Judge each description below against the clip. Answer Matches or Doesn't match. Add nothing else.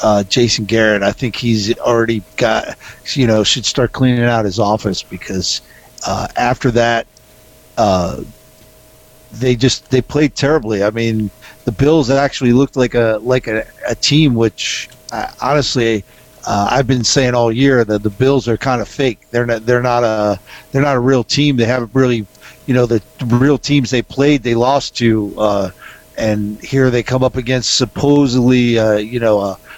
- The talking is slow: Doesn't match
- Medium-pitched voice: Doesn't match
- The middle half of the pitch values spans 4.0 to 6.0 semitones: Doesn't match